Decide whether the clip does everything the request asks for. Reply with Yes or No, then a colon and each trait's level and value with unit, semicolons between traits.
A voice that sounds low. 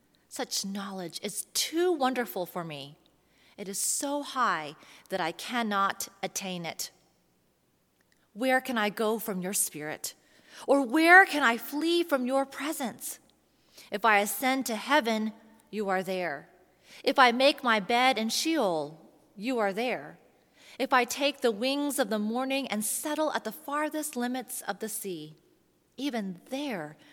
No: high, 240 Hz